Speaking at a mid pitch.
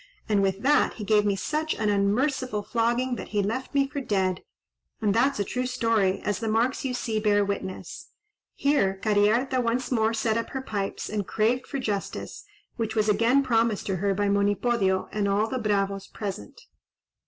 No: high, 220 Hz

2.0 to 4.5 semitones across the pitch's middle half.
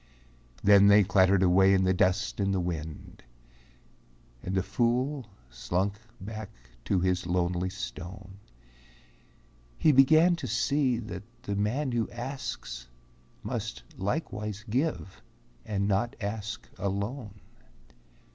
Yes: average, 4.1 semitones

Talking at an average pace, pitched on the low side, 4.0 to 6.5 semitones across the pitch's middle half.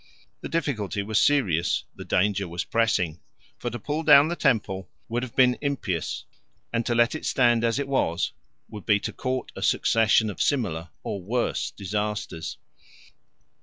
Yes: average, 165 wpm; low, 115 Hz; average, 4.6 semitones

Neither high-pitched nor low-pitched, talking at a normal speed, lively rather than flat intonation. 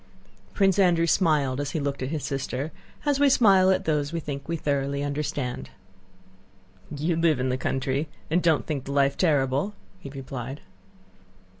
No: medium, 145 Hz; average, 165 wpm; average, 3.5 semitones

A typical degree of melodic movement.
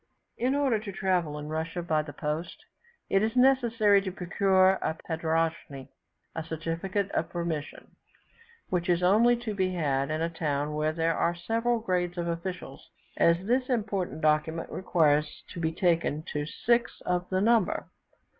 Yes: average, 4.0 semitones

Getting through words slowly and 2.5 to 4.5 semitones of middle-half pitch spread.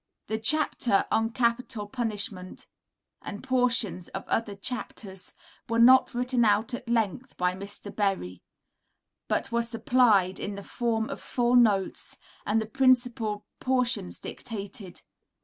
Yes: slow, 130 wpm; average, 3.4 semitones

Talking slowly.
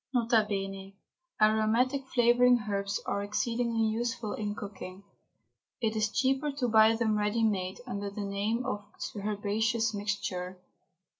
Yes: slow, 125 wpm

